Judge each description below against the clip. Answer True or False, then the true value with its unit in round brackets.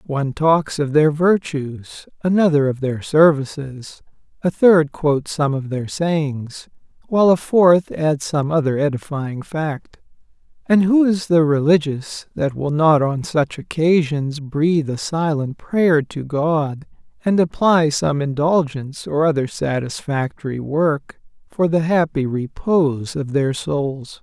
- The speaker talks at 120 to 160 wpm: True (140 wpm)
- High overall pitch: False (150 Hz)